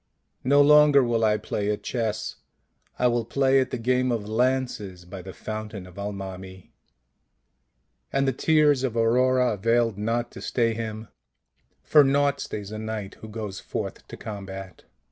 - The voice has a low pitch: Yes, low, 115 Hz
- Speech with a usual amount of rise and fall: Yes, average, 3.8 semitones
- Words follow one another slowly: No, average, 165 wpm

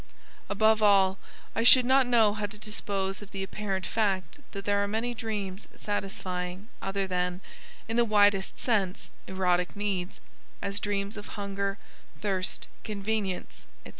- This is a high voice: Yes, high, 200 Hz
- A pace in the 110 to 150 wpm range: Yes, average, 145 wpm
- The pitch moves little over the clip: Yes, narrow, 1.9 semitones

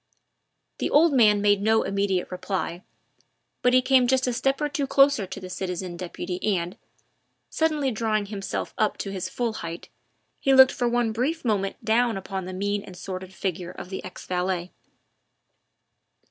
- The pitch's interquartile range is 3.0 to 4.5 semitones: No, average, 5.1 semitones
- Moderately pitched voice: No, high, 205 Hz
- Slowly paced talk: No, average, 170 wpm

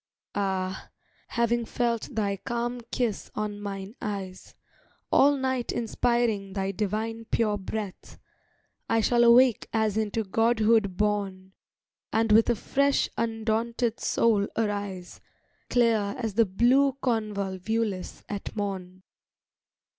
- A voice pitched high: Yes, high, 220 Hz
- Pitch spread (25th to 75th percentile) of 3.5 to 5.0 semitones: No, average, 2.8 semitones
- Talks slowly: Yes, slow, 110 wpm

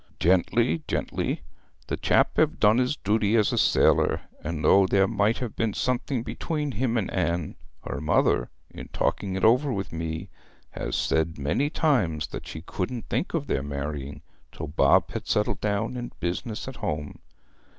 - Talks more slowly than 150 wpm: No, average, 170 wpm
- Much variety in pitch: Yes, wide, 7.0 semitones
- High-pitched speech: No, low, 100 Hz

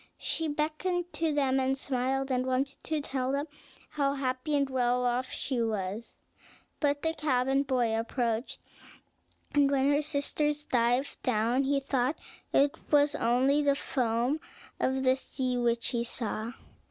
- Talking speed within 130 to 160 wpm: Yes, average, 150 wpm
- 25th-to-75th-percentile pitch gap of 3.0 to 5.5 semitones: No, narrow, 2.6 semitones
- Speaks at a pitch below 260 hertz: No, very high, 265 Hz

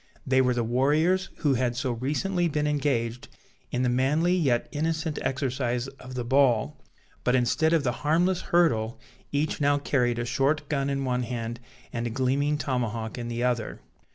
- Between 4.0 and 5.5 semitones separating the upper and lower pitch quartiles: No, average, 3.6 semitones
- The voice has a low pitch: Yes, low, 130 Hz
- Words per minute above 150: Yes, average, 175 wpm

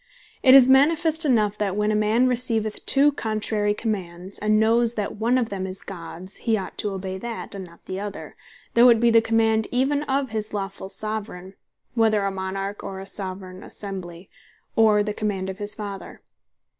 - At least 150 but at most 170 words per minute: No, average, 185 wpm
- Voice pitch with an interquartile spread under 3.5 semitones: Yes, average, 2.9 semitones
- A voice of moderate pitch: No, high, 210 Hz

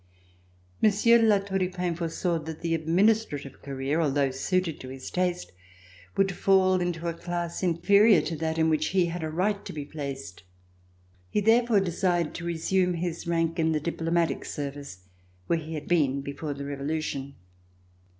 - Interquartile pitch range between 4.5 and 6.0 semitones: No, average, 3.4 semitones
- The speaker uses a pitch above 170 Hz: No, medium, 165 Hz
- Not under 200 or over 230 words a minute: No, average, 170 wpm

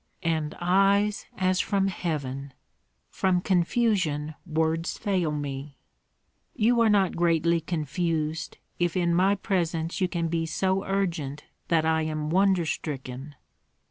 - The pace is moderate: No, slow, 125 wpm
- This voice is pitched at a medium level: Yes, medium, 170 Hz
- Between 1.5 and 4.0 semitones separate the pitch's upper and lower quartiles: Yes, average, 3.5 semitones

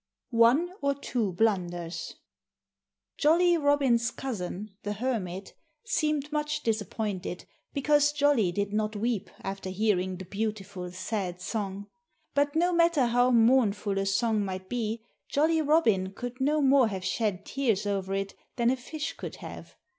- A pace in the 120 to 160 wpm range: Yes, average, 145 wpm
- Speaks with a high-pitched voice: Yes, high, 225 Hz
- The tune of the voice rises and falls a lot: Yes, wide, 6.2 semitones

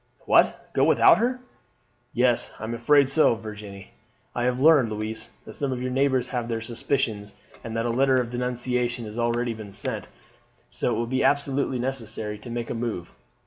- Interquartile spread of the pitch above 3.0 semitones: No, average, 2.7 semitones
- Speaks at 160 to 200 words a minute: Yes, average, 185 wpm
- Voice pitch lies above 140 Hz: No, low, 120 Hz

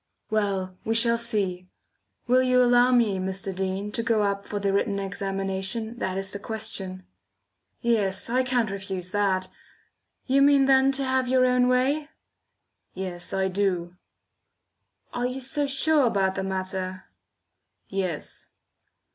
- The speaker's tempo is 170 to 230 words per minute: No, average, 140 wpm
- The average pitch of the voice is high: Yes, high, 205 Hz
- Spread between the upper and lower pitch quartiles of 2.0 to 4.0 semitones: No, average, 4.7 semitones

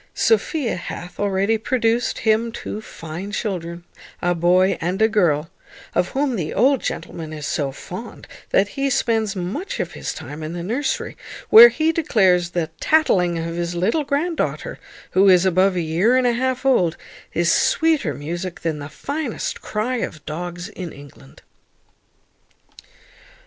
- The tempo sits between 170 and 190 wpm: No, average, 155 wpm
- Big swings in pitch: Yes, wide, 6.4 semitones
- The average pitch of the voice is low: No, high, 190 Hz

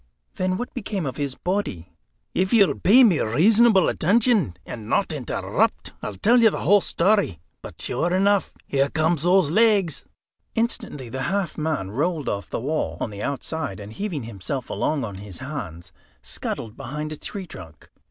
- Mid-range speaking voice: Yes, medium, 155 Hz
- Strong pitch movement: Yes, wide, 8.7 semitones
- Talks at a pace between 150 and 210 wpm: Yes, average, 170 wpm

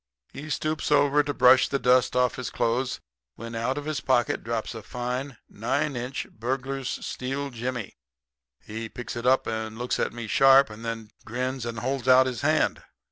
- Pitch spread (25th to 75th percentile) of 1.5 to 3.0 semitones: Yes, narrow, 2.6 semitones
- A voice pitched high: No, low, 125 Hz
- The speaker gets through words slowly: No, average, 185 wpm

